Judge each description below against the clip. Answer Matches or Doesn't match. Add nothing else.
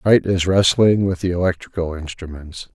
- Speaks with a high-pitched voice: Doesn't match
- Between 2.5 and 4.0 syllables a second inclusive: Doesn't match